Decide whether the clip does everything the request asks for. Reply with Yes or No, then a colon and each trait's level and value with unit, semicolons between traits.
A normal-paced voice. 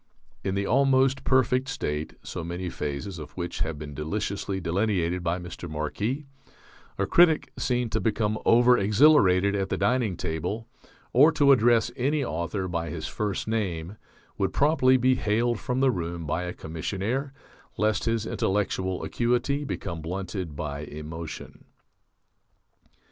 Yes: average, 145 wpm